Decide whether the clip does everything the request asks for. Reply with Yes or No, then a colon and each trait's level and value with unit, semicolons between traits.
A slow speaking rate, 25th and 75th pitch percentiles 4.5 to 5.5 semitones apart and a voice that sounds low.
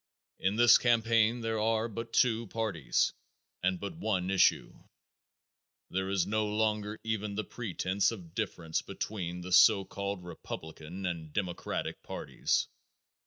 No: slow, 130 wpm; average, 3.3 semitones; low, 100 Hz